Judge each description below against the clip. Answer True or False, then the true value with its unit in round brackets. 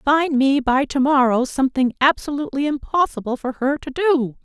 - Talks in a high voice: True (275 Hz)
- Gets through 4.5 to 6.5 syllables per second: True (5.2 syllables/s)